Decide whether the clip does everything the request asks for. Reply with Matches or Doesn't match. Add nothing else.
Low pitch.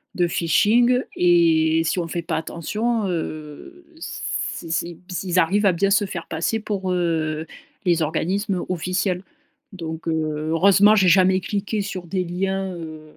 Doesn't match